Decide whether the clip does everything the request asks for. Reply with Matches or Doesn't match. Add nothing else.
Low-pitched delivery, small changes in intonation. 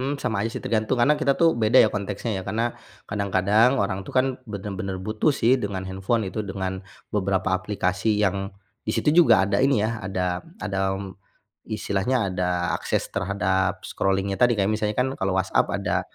Doesn't match